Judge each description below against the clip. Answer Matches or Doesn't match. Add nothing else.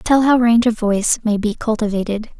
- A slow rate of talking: Doesn't match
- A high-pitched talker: Matches